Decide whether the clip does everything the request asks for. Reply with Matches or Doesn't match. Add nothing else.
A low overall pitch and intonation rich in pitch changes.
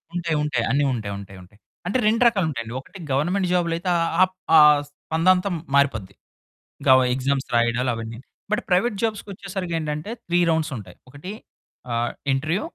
Doesn't match